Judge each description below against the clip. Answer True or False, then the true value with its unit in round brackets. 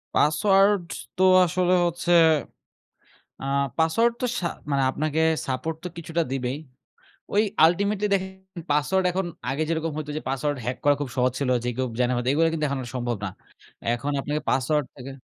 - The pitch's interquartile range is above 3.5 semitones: True (5.0 semitones)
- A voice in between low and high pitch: True (155 Hz)